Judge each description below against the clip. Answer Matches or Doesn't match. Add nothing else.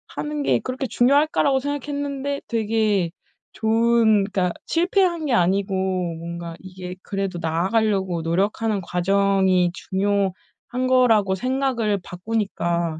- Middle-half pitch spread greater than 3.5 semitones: Matches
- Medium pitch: Doesn't match